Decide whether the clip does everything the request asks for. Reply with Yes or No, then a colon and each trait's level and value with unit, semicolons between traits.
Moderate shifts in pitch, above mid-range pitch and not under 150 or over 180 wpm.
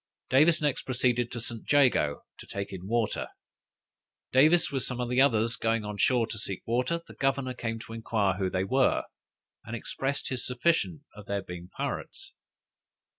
No: average, 3.9 semitones; low, 120 Hz; average, 165 wpm